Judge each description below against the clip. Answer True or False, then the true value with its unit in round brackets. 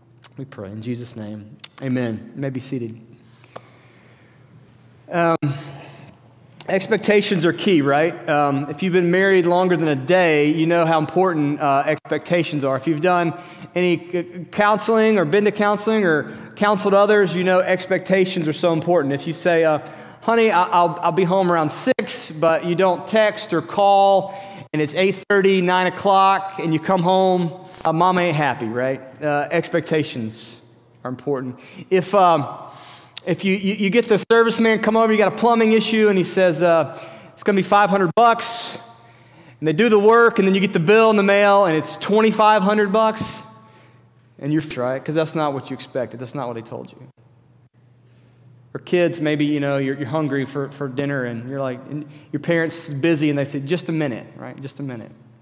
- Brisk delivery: False (190 wpm)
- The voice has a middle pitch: True (165 Hz)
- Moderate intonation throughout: False (5.8 semitones)